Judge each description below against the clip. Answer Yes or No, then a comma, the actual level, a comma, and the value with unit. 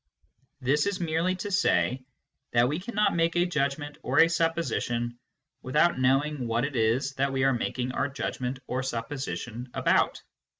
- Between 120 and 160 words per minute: No, average, 170 wpm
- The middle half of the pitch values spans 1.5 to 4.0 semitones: No, average, 4.6 semitones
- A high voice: No, low, 135 Hz